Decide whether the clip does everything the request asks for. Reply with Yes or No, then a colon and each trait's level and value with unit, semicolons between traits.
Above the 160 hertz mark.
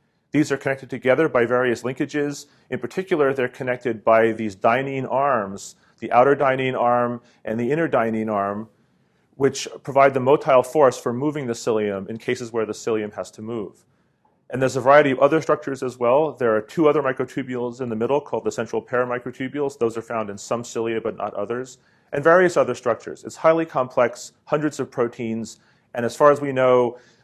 No: low, 125 Hz